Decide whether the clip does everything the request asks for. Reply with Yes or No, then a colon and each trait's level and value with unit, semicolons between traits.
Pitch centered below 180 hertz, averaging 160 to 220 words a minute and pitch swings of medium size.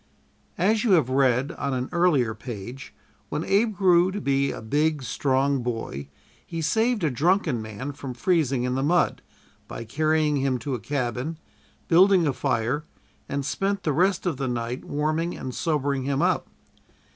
Yes: medium, 140 Hz; average, 170 wpm; average, 5.0 semitones